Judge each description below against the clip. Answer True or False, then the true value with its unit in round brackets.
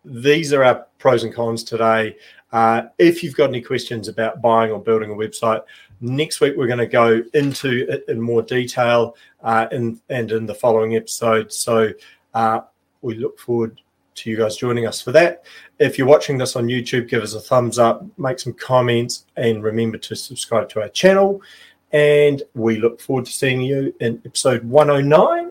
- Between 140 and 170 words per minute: False (190 wpm)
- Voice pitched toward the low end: True (120 Hz)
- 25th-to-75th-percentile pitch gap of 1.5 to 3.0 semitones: True (2.5 semitones)